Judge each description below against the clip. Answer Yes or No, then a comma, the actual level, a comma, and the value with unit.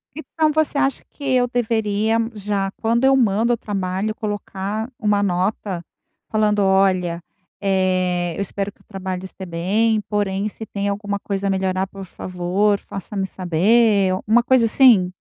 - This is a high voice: Yes, high, 200 Hz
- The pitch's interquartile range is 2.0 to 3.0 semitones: Yes, average, 2.7 semitones